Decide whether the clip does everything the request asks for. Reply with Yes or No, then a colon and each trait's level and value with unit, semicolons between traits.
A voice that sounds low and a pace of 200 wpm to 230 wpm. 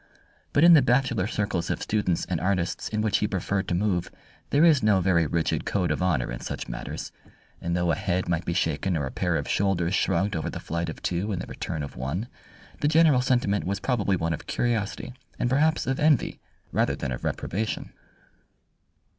Yes: very low, 95 Hz; fast, 205 wpm